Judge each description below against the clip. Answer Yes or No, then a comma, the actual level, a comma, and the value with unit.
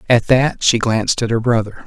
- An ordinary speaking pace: No, fast, 225 wpm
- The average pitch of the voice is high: No, low, 115 Hz